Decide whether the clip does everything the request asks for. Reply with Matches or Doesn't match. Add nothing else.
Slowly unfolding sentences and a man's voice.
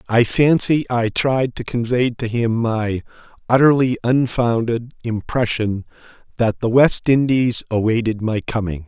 Matches